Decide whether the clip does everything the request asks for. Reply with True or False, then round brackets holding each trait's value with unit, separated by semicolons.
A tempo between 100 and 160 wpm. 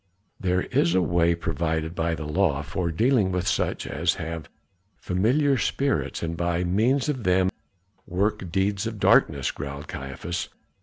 True (150 wpm)